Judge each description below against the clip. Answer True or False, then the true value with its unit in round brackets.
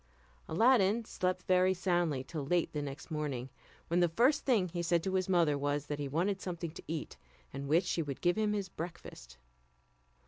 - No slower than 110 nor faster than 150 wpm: False (195 wpm)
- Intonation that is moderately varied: True (4.1 semitones)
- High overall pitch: False (170 Hz)